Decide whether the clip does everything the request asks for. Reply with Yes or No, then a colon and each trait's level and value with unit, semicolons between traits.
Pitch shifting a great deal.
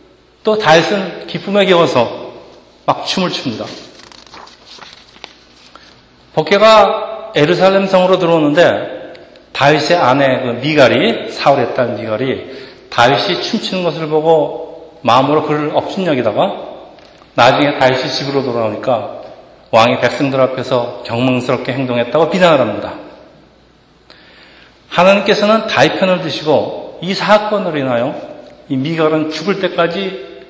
Yes: wide, 6.3 semitones